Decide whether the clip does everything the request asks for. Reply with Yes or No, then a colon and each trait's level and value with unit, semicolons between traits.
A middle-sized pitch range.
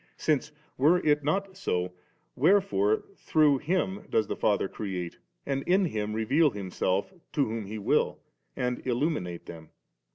No: wide, 7.6 semitones